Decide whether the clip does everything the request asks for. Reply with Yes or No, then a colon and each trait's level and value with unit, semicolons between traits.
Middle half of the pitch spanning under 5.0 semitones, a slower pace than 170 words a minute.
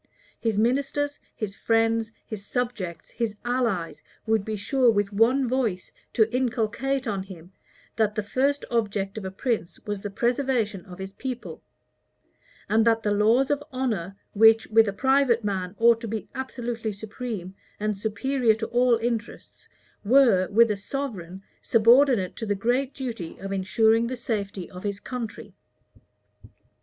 Yes: average, 3.5 semitones; average, 150 wpm